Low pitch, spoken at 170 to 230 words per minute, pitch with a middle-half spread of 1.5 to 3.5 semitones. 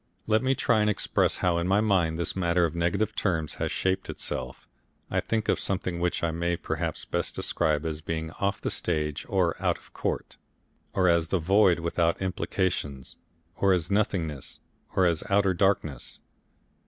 Yes: very low, 90 Hz; average, 175 wpm; average, 3.0 semitones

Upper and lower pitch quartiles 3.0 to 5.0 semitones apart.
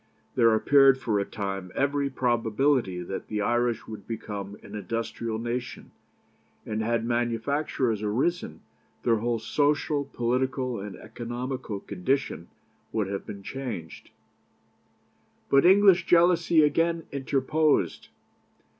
Yes: average, 4.6 semitones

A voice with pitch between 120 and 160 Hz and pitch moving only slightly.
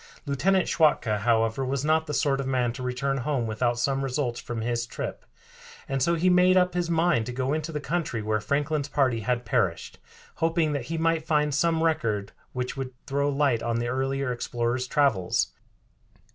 No: low, 135 Hz; average, 4.4 semitones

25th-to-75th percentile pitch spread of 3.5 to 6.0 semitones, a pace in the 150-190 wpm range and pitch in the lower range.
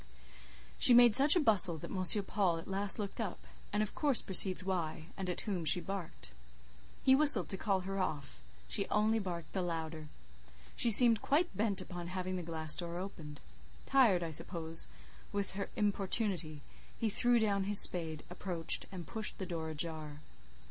No: average, 4.0 semitones; average, 175 wpm; medium, 185 Hz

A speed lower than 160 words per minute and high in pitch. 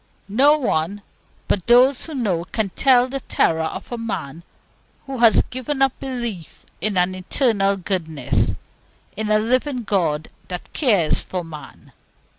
Yes: average, 145 wpm; high, 215 Hz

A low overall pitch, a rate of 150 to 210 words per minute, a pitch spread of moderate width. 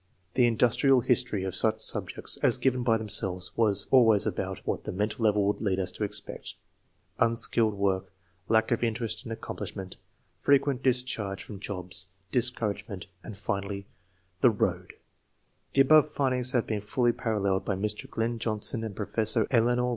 Yes: low, 110 Hz; average, 160 wpm; average, 3.4 semitones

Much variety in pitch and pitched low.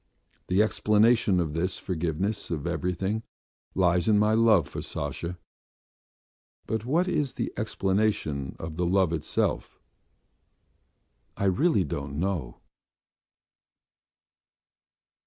No: average, 4.3 semitones; very low, 95 Hz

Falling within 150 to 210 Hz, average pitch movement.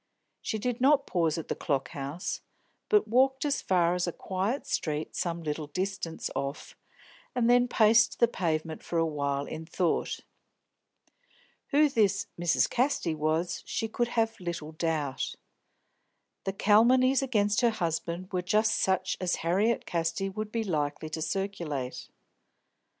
No: medium, 185 Hz; wide, 5.8 semitones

